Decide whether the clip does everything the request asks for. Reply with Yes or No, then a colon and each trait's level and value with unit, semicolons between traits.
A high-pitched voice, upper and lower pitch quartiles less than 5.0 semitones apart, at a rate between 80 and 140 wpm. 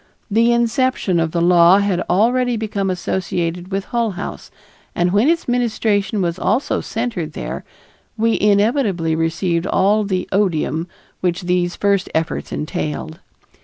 Yes: high, 195 Hz; average, 4.3 semitones; slow, 135 wpm